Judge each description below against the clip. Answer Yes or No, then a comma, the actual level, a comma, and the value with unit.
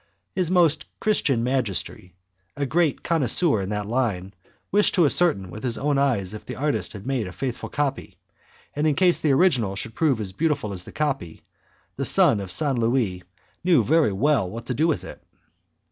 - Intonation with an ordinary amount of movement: No, wide, 6.6 semitones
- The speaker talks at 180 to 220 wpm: Yes, average, 190 wpm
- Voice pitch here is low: Yes, low, 130 Hz